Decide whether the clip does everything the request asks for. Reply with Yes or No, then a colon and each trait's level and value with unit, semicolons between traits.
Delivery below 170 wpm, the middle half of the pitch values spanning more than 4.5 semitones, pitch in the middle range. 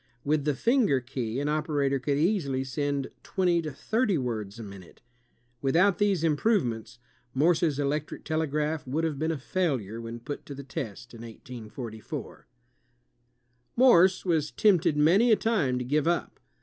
Yes: average, 150 wpm; average, 4.9 semitones; medium, 150 Hz